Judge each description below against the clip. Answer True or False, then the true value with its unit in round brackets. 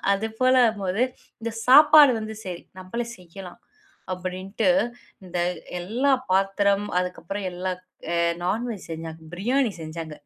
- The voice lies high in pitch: True (195 Hz)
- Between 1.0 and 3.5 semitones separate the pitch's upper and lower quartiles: False (4.0 semitones)